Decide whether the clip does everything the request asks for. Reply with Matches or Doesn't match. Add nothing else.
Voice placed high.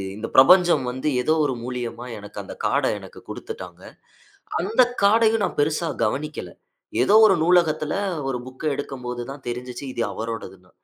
Doesn't match